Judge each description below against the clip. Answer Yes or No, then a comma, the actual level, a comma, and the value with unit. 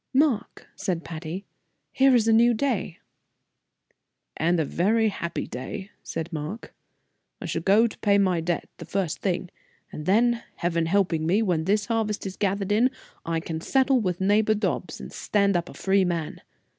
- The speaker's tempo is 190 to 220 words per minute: No, average, 170 wpm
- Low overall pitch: No, high, 195 Hz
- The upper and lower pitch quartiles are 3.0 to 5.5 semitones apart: Yes, average, 4.3 semitones